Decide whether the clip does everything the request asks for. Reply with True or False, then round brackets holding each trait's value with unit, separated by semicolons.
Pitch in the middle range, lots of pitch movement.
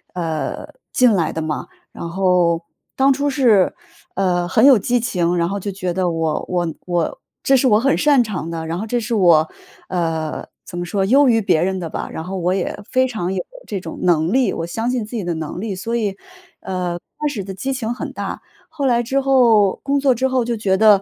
False (195 Hz; 5.7 semitones)